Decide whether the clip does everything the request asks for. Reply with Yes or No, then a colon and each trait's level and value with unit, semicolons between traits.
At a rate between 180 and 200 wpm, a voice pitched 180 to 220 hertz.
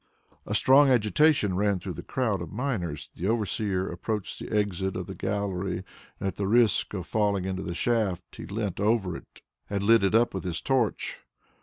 No: average, 185 wpm; low, 100 Hz